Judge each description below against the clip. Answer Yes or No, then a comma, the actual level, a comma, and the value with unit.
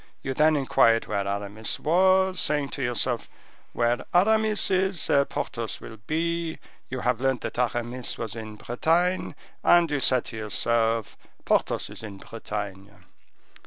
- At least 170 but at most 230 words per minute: No, average, 145 wpm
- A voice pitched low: Yes, low, 125 Hz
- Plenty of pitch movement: Yes, wide, 6.6 semitones